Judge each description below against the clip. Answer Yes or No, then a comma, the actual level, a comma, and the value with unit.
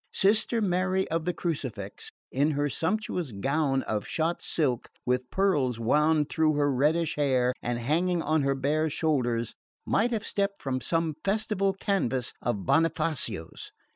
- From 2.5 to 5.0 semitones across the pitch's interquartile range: No, wide, 5.4 semitones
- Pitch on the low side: No, medium, 155 Hz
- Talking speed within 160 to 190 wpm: No, average, 145 wpm